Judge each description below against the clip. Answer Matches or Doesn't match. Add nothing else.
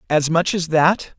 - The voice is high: Doesn't match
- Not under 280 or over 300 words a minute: Doesn't match